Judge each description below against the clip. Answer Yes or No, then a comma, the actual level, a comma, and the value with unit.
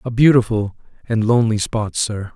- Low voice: Yes, low, 110 Hz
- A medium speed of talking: Yes, average, 155 wpm